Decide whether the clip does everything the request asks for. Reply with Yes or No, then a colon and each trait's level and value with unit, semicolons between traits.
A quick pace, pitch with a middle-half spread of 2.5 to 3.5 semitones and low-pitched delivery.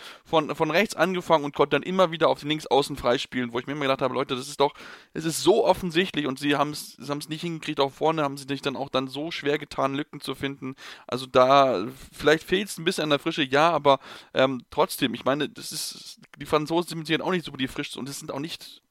No: fast, 260 wpm; average, 2.9 semitones; medium, 145 Hz